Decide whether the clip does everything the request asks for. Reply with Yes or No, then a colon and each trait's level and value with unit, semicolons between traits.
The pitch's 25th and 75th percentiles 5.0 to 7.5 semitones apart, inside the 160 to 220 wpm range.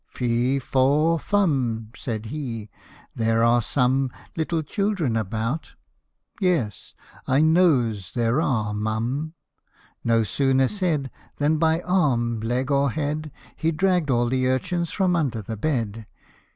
No: wide, 5.4 semitones; average, 140 wpm